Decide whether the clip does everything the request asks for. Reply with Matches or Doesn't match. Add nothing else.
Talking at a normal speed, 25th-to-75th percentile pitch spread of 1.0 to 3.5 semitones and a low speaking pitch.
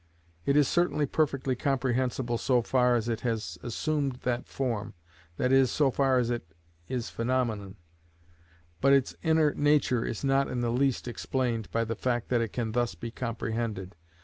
Matches